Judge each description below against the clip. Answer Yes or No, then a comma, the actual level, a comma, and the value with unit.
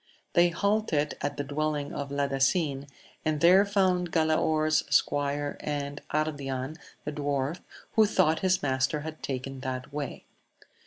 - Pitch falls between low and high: Yes, medium, 145 Hz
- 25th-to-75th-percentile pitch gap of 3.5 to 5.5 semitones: No, narrow, 2.4 semitones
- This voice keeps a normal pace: No, slow, 130 wpm